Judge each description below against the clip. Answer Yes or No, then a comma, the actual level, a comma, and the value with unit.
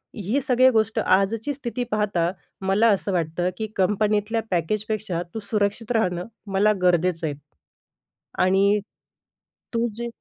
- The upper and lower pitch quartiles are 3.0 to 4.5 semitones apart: Yes, average, 3.3 semitones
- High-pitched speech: Yes, high, 205 Hz